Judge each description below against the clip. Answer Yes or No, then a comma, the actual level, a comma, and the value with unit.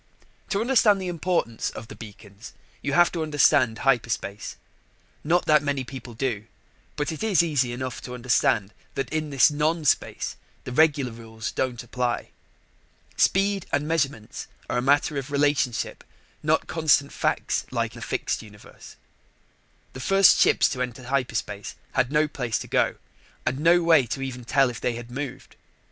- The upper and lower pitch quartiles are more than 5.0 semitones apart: No, average, 4.2 semitones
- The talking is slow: No, average, 160 wpm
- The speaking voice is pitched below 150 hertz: Yes, low, 135 Hz